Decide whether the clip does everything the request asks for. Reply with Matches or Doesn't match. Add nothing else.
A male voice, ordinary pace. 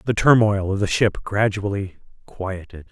Matches